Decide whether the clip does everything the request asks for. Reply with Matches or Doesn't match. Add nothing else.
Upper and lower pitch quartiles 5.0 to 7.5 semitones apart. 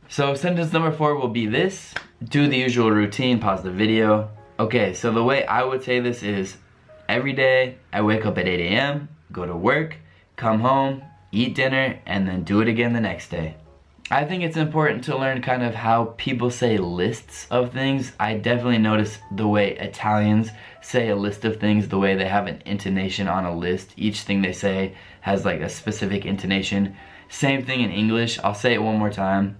Doesn't match